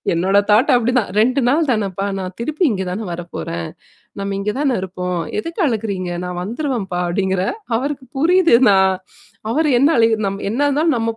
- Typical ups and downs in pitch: No, wide, 6.1 semitones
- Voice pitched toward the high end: Yes, high, 215 Hz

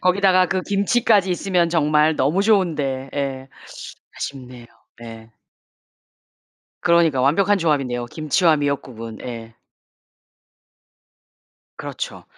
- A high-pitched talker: No, medium, 150 Hz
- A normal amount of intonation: No, wide, 5.8 semitones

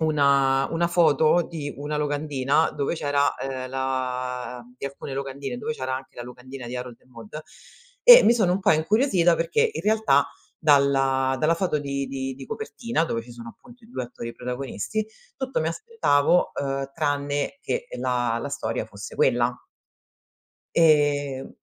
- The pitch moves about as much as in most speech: Yes, average, 4.1 semitones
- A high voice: No, medium, 140 Hz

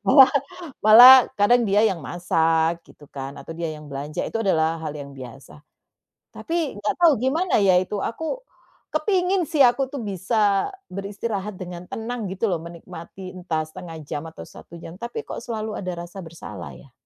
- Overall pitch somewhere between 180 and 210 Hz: Yes, medium, 185 Hz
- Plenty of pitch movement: Yes, wide, 6.2 semitones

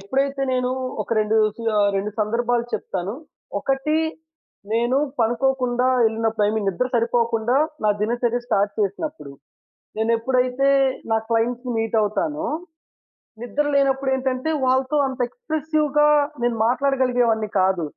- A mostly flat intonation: No, average, 3.2 semitones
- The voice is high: Yes, high, 245 Hz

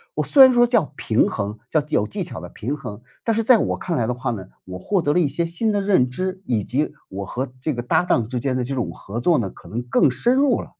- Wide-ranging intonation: Yes, wide, 8.0 semitones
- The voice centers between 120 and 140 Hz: Yes, low, 135 Hz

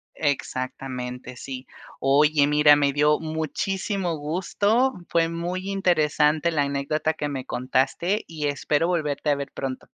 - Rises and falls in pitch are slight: No, average, 3.1 semitones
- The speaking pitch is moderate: Yes, medium, 150 Hz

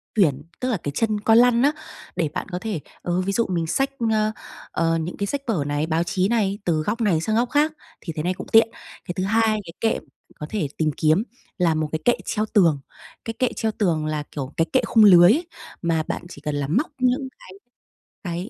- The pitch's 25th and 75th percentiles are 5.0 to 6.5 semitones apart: Yes, wide, 5.6 semitones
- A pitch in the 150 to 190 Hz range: Yes, medium, 185 Hz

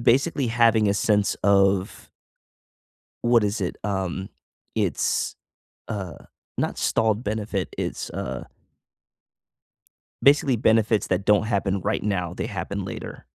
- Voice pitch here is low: Yes, low, 105 Hz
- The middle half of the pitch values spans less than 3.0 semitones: Yes, narrow, 2.5 semitones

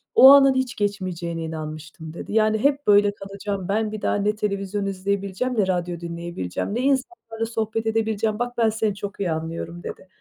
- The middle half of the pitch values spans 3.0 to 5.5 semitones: Yes, average, 3.9 semitones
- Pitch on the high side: Yes, high, 205 Hz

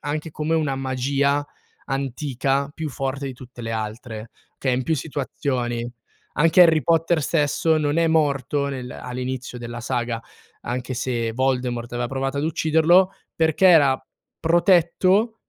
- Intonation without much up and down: No, average, 4.2 semitones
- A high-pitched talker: No, medium, 140 Hz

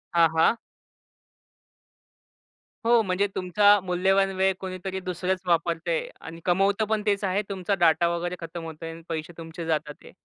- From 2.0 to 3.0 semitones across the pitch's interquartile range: Yes, narrow, 2.6 semitones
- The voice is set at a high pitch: No, medium, 180 Hz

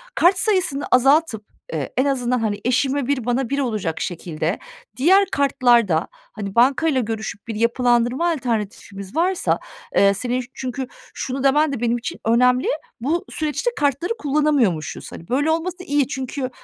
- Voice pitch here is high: Yes, very high, 255 Hz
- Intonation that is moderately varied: Yes, average, 3.9 semitones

